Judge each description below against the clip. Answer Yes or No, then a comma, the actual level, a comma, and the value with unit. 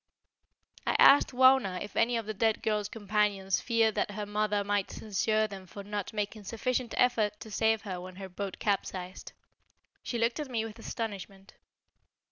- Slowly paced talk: No, average, 170 wpm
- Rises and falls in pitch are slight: Yes, narrow, 2.3 semitones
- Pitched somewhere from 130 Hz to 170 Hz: No, high, 210 Hz